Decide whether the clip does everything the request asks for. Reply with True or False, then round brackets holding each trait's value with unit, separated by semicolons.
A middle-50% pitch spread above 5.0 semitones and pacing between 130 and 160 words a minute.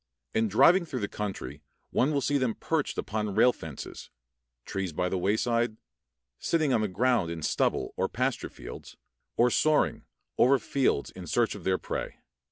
False (5.6 semitones; 170 wpm)